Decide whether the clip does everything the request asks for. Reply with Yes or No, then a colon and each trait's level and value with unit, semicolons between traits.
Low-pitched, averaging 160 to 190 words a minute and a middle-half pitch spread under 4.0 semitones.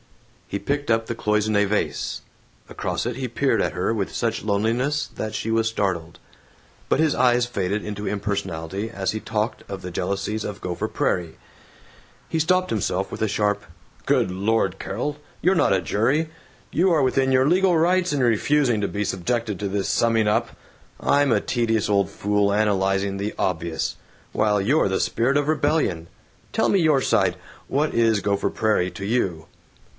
No: low, 110 Hz; average, 170 wpm; average, 4.8 semitones